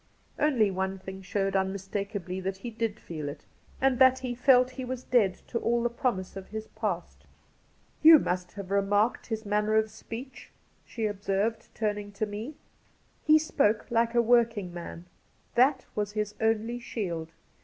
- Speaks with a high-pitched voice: Yes, high, 215 Hz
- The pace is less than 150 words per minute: No, average, 175 wpm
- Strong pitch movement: No, average, 3.6 semitones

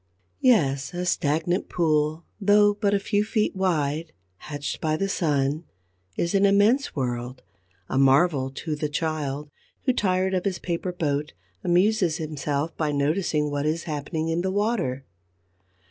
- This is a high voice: No, medium, 160 Hz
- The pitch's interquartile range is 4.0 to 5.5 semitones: Yes, average, 4.6 semitones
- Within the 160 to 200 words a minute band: No, average, 145 wpm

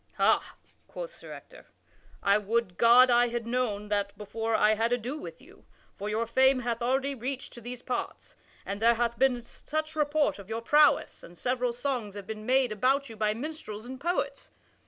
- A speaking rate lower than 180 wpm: No, average, 190 wpm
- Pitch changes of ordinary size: Yes, average, 3.4 semitones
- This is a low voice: No, high, 240 Hz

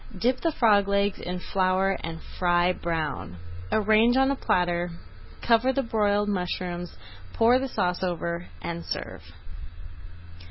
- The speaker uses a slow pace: Yes, slow, 130 wpm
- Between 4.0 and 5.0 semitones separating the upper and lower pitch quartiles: Yes, average, 4.3 semitones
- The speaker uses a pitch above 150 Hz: Yes, high, 190 Hz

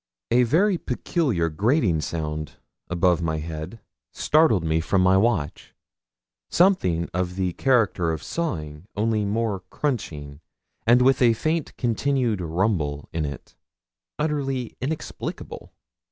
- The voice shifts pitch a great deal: Yes, wide, 7.7 semitones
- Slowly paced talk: Yes, slow, 120 wpm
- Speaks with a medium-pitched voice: No, low, 100 Hz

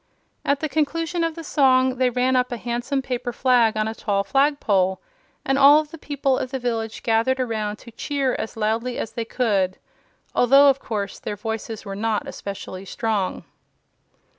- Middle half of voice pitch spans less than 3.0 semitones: No, average, 3.7 semitones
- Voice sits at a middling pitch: No, high, 245 Hz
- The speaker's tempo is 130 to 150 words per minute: No, average, 180 wpm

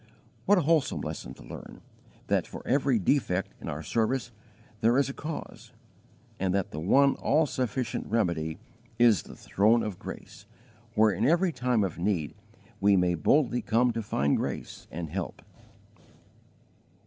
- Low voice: Yes, low, 110 Hz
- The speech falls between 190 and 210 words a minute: No, average, 155 wpm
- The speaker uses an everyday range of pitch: No, wide, 6.5 semitones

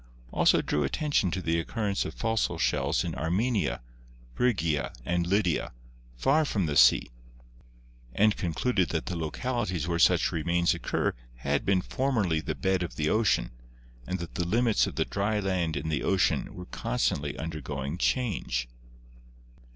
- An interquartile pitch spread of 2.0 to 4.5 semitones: No, average, 5.0 semitones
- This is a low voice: Yes, very low, 85 Hz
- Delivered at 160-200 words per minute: No, average, 150 wpm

